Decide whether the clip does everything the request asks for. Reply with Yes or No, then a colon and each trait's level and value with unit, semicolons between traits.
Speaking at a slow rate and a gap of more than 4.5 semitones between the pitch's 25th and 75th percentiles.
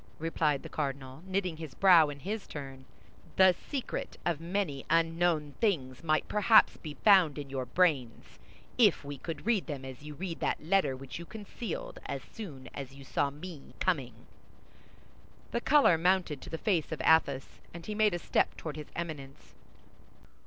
No: average, 170 wpm; average, 5.1 semitones